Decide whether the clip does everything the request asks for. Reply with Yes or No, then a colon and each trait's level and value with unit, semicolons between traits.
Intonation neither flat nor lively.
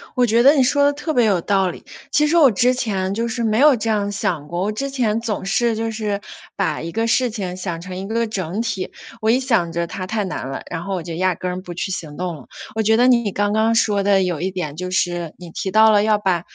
Yes: average, 4.0 semitones